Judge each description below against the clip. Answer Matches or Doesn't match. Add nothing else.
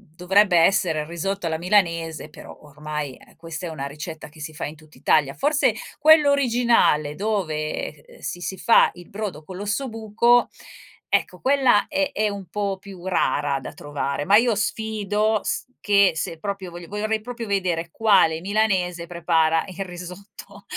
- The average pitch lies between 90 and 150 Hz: Doesn't match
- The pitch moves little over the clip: Doesn't match